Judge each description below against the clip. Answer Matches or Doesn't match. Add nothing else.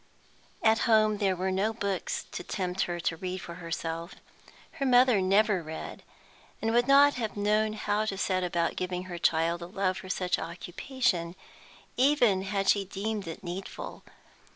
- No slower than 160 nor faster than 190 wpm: Matches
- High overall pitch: Matches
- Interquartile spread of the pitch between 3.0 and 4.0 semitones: Matches